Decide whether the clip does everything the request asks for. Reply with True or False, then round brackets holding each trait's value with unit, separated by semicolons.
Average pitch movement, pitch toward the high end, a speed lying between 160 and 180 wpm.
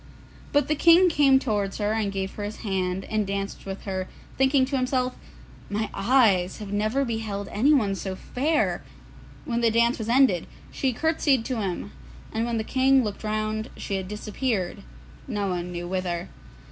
True (4.8 semitones; 215 Hz; 170 wpm)